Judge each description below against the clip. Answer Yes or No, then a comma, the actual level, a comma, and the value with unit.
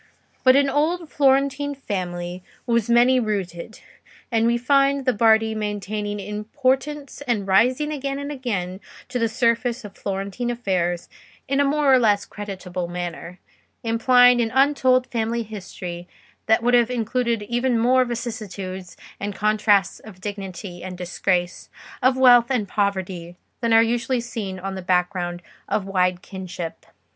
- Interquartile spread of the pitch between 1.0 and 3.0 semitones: No, average, 4.8 semitones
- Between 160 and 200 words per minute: No, average, 145 wpm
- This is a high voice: Yes, high, 225 Hz